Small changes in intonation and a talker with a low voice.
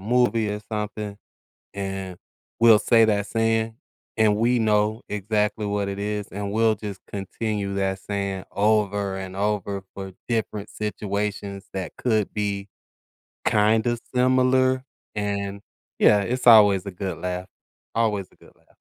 Yes: narrow, 2.0 semitones; low, 105 Hz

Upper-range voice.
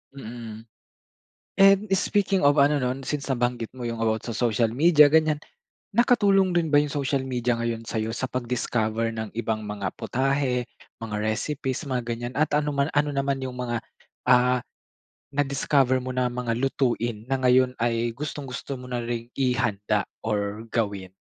No: low, 125 Hz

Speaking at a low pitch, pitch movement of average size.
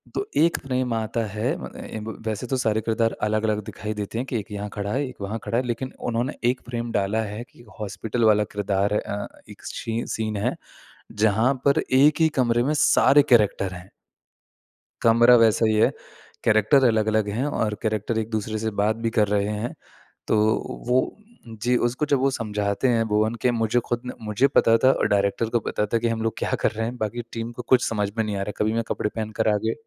No: low, 110 Hz; narrow, 2.2 semitones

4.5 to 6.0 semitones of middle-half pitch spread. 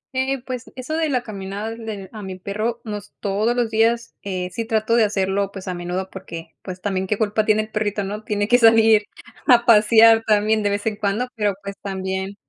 No: narrow, 2.5 semitones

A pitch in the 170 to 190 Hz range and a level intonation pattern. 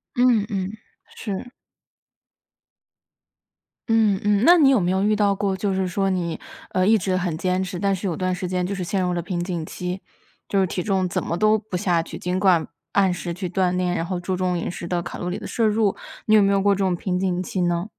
Yes: medium, 185 Hz; narrow, 1.9 semitones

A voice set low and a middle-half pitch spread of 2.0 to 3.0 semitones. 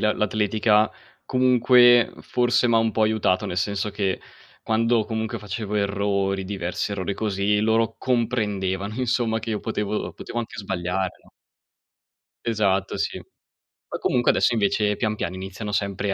Yes: low, 105 Hz; narrow, 2.4 semitones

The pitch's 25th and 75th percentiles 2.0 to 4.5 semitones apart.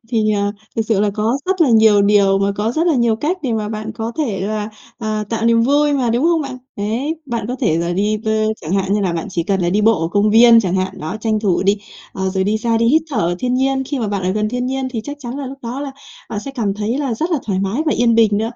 Yes: average, 3.8 semitones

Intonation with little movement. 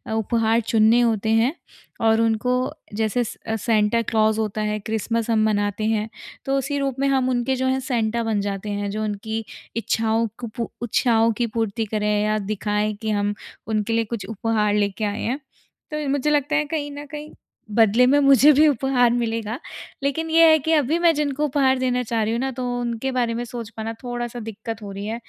No: average, 3.2 semitones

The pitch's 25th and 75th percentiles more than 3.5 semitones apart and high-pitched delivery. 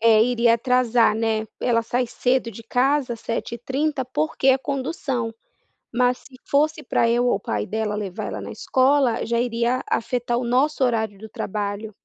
No: narrow, 2.4 semitones; high, 240 Hz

